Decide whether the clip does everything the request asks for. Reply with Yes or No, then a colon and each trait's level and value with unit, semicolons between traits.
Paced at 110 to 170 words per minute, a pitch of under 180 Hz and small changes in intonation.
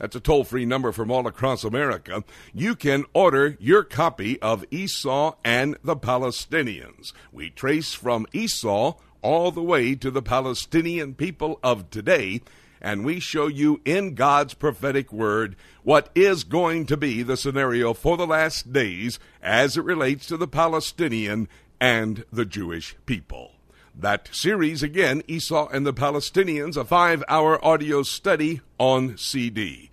No: average, 150 wpm; medium, 140 Hz; average, 4.4 semitones